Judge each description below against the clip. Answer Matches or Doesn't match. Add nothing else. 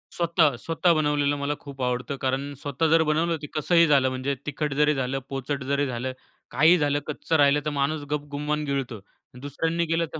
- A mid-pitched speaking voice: Matches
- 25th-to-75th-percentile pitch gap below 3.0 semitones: Matches